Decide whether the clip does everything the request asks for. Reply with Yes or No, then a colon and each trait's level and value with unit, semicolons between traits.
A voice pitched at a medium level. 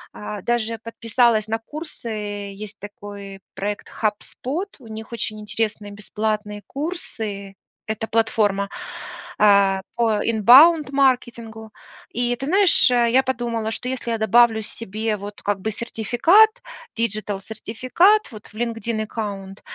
No: high, 220 Hz